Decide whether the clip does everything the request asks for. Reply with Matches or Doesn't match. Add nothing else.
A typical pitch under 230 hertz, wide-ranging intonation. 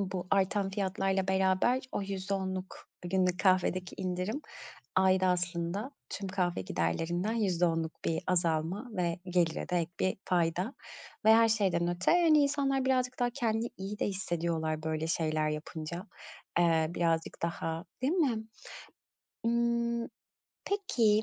Doesn't match